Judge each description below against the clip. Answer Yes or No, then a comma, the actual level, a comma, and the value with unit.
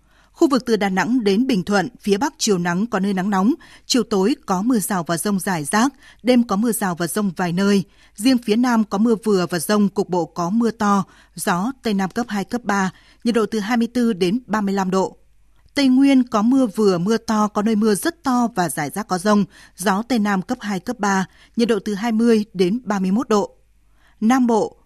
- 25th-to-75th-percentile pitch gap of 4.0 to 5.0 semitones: No, average, 3.5 semitones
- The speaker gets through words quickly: No, average, 225 wpm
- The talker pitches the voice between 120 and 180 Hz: No, high, 210 Hz